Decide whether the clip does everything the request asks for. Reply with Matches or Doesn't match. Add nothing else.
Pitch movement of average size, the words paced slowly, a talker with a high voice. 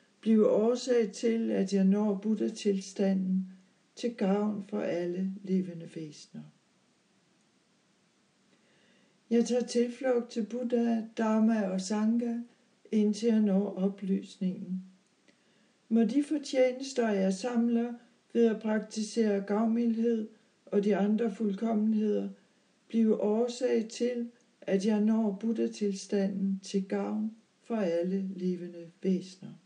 Matches